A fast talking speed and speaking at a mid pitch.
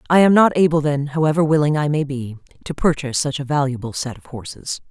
Yes: fast, 220 wpm; medium, 145 Hz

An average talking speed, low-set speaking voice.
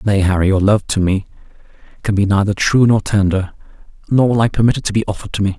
No: fast, 225 wpm; low, 105 Hz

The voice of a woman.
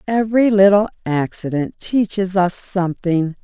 Yes: female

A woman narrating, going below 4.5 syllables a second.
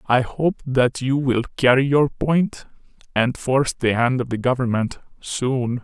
Yes: female; 4.2 syllables/s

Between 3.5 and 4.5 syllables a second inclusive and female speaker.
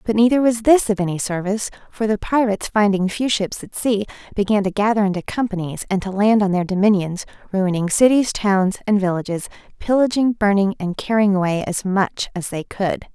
No: 5.4 syllables/s; female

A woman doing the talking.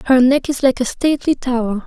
Yes: female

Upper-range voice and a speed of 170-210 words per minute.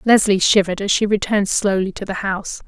Yes: high, 200 Hz; average, 200 wpm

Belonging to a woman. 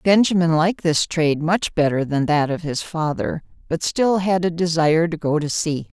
Yes: female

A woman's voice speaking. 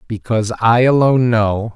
No: male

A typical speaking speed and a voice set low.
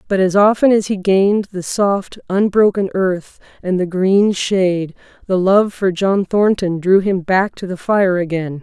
No: average, 180 wpm; high, 190 Hz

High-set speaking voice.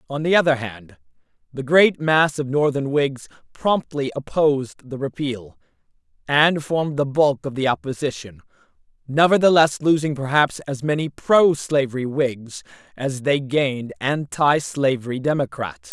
No: medium, 140 Hz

